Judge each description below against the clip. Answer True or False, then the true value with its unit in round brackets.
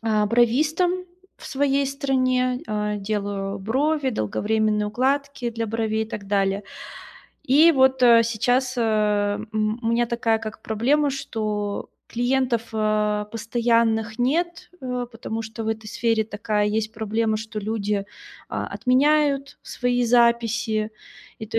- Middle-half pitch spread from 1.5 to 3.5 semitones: True (3.1 semitones)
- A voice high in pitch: True (230 Hz)